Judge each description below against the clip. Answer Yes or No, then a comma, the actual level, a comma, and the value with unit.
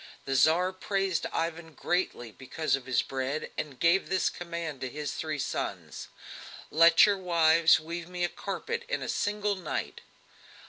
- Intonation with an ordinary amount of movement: Yes, average, 3.3 semitones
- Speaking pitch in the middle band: Yes, medium, 165 Hz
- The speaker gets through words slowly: No, average, 155 wpm